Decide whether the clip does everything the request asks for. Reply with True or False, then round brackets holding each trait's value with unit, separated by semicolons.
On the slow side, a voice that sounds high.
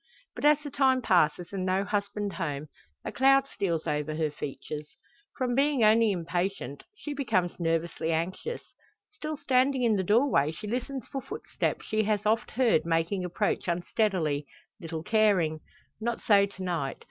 False (160 wpm; 200 Hz)